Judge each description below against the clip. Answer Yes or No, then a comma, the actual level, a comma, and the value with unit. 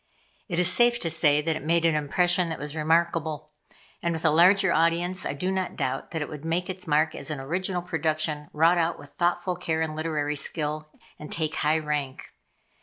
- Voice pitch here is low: No, medium, 160 Hz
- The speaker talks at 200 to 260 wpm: Yes, fast, 205 wpm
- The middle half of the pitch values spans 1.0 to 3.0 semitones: Yes, narrow, 2.4 semitones